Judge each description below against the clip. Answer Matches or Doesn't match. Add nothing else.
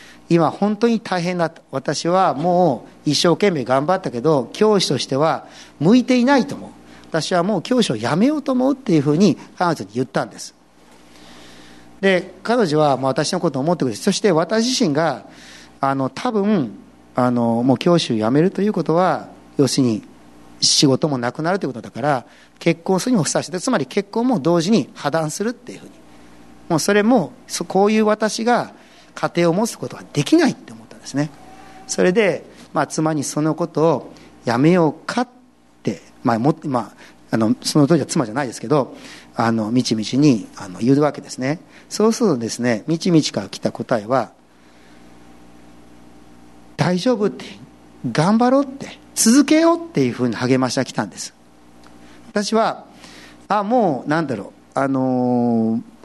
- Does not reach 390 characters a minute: Matches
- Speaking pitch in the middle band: Matches